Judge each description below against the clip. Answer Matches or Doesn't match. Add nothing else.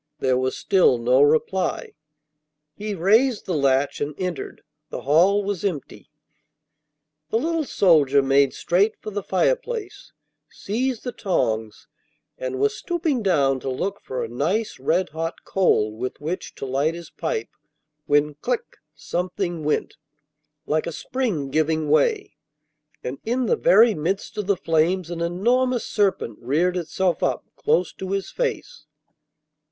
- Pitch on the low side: Doesn't match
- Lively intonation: Matches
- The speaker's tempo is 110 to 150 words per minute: Matches